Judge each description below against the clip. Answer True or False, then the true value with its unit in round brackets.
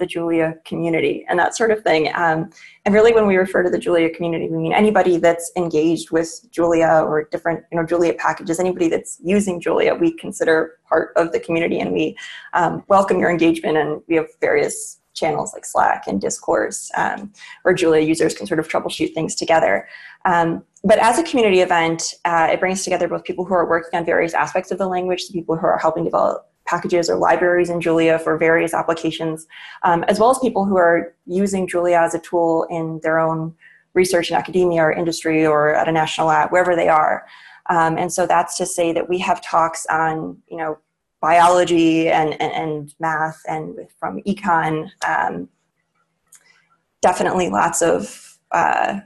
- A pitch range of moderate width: False (2.0 semitones)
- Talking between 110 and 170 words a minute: False (190 wpm)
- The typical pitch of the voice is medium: True (170 Hz)